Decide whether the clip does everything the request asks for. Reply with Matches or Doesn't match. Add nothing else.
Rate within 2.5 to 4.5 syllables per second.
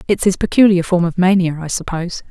Doesn't match